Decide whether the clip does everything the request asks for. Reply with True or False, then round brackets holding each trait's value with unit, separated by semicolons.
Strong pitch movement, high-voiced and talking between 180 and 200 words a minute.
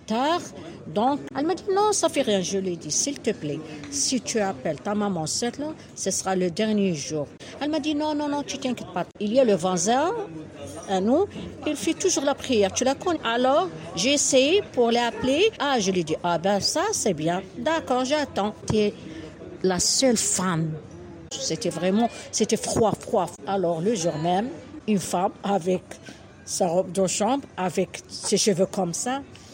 True (7.1 semitones; 210 Hz; 185 wpm)